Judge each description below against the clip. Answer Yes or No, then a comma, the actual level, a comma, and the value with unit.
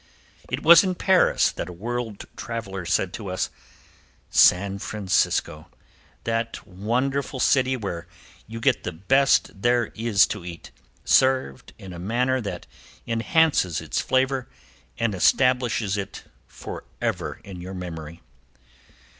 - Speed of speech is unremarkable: No, slow, 125 wpm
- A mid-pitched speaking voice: No, low, 115 Hz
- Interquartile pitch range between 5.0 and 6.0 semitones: Yes, wide, 5.6 semitones